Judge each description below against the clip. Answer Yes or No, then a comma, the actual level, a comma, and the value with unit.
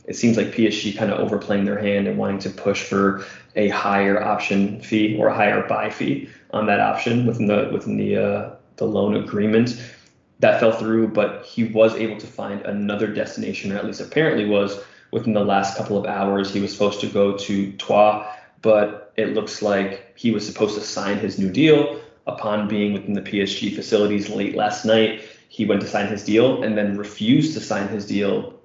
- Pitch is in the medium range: No, low, 105 Hz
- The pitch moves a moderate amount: No, narrow, 1.4 semitones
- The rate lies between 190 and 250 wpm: Yes, fast, 205 wpm